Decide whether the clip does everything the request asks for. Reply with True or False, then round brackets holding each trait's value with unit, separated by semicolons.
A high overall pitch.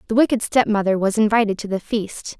True (215 Hz)